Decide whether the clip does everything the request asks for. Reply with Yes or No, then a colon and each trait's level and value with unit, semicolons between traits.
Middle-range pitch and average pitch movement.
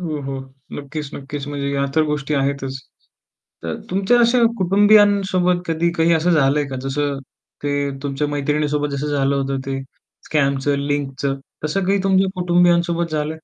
Yes: medium, 150 Hz; average, 3.8 semitones